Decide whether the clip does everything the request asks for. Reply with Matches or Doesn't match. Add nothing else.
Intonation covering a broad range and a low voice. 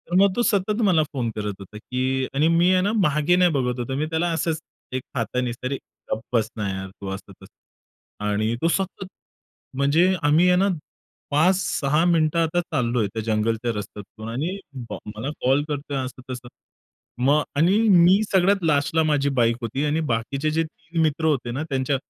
Doesn't match